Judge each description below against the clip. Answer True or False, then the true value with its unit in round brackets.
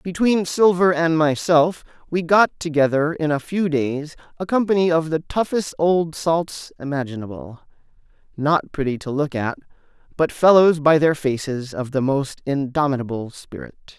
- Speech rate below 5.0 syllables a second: True (4.6 syllables/s)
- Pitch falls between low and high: True (155 Hz)